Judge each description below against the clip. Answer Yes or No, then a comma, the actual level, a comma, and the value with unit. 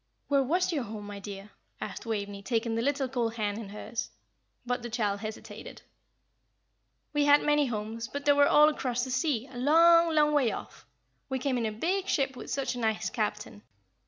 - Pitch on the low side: No, high, 245 Hz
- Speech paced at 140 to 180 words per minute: No, average, 195 wpm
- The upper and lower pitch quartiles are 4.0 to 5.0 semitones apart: Yes, average, 4.6 semitones